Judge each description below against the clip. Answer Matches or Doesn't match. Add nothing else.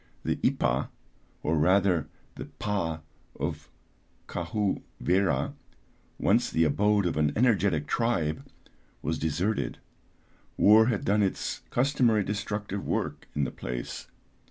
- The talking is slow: Matches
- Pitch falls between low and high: Doesn't match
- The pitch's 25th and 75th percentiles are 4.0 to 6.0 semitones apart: Matches